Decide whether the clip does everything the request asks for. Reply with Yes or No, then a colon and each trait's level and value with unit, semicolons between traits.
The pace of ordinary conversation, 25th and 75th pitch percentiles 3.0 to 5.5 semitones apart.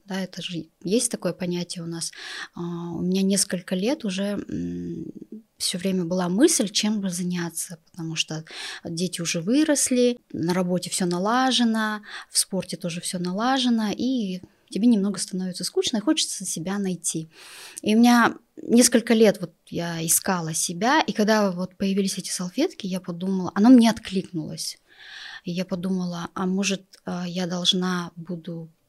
Yes: average, 145 wpm; average, 3.8 semitones